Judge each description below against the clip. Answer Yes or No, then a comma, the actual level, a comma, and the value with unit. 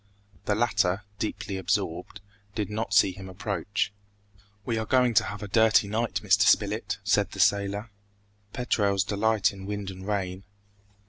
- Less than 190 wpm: Yes, average, 150 wpm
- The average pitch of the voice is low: Yes, low, 100 Hz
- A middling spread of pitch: No, narrow, 2.0 semitones